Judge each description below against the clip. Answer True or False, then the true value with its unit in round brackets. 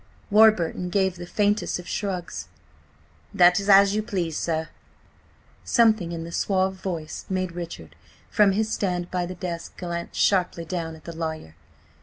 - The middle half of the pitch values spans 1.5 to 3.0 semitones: True (2.7 semitones)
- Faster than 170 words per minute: False (155 wpm)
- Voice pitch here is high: False (180 Hz)